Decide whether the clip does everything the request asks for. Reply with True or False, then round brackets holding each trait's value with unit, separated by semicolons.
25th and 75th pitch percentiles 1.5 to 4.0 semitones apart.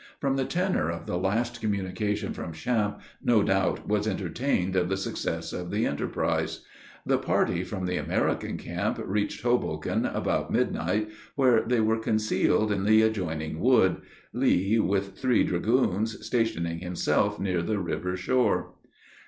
True (3.6 semitones)